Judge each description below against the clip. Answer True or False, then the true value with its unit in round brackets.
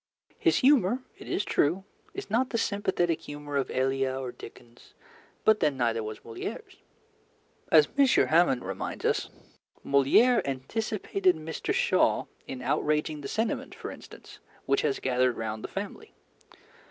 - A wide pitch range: True (8.3 semitones)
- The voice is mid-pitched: True (150 Hz)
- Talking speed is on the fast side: False (140 wpm)